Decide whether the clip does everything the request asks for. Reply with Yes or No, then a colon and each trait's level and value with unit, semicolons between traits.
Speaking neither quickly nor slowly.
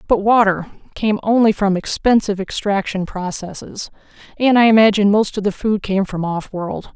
Yes: average, 155 wpm